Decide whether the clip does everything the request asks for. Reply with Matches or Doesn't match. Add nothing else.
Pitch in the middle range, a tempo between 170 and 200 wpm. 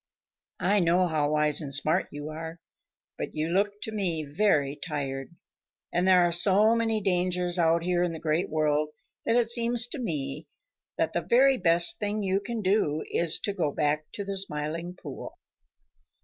Matches